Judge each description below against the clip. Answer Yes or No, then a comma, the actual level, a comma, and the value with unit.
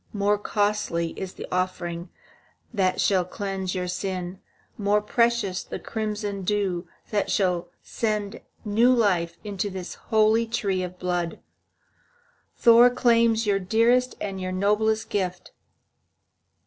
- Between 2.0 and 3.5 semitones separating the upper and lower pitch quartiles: Yes, average, 3.0 semitones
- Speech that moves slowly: Yes, slow, 120 wpm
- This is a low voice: No, high, 200 Hz